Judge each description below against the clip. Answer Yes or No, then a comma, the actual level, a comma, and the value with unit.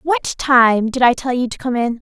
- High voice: Yes, very high, 255 Hz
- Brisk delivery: Yes, fast, 255 wpm